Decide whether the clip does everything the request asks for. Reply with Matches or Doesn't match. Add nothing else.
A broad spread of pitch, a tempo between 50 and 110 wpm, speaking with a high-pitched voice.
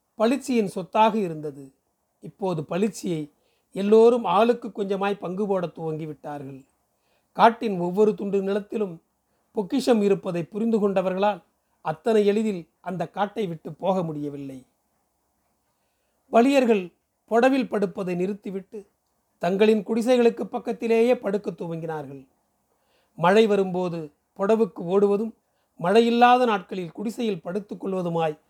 Doesn't match